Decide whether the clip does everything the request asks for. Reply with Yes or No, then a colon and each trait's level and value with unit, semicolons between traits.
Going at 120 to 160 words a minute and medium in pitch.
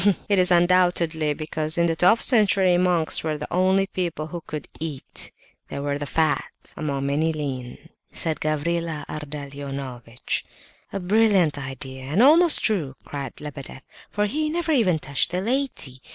Yes: average, 150 wpm; medium, 160 Hz